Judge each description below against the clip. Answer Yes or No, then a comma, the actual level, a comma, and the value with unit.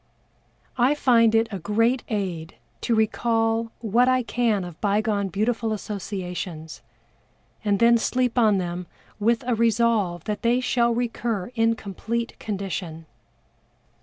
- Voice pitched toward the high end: Yes, high, 220 Hz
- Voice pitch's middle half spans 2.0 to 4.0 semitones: Yes, average, 3.0 semitones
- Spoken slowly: Yes, slow, 130 wpm